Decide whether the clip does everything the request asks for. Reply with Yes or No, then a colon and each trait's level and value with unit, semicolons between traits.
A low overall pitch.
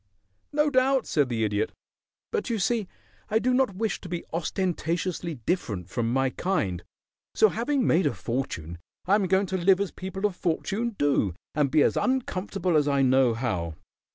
No: medium, 180 Hz